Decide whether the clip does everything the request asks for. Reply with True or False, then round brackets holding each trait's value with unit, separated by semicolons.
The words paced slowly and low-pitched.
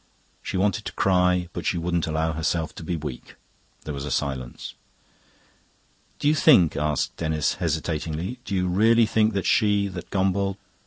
False (160 wpm; 90 Hz)